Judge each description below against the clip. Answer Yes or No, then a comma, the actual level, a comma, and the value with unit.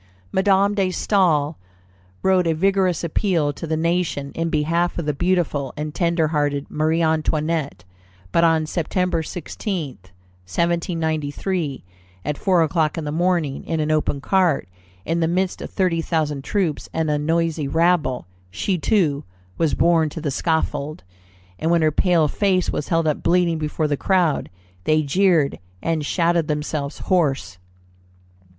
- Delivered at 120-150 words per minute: Yes, average, 145 wpm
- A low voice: No, medium, 160 Hz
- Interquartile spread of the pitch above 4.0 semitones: No, average, 2.8 semitones